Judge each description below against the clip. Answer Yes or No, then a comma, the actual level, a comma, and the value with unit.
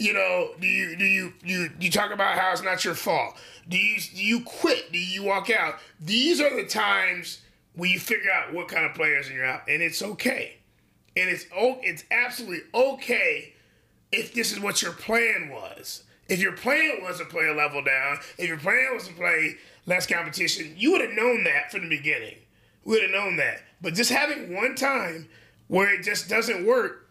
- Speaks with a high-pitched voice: Yes, high, 195 Hz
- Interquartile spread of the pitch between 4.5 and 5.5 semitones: Yes, average, 5.1 semitones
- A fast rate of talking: Yes, fast, 210 wpm